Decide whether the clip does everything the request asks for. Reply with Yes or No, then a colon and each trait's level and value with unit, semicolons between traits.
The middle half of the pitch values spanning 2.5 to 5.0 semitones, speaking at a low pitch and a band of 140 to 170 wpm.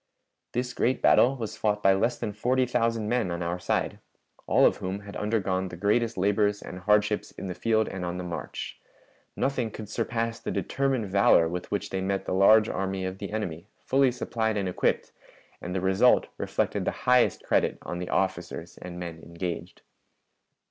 No: average, 3.7 semitones; low, 100 Hz; average, 185 wpm